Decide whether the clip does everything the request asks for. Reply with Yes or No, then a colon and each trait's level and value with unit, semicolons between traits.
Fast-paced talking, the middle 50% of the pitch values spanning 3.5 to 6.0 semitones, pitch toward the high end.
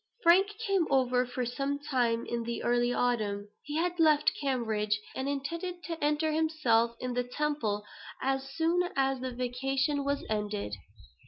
No: average, 155 wpm; average, 4.1 semitones; very high, 270 Hz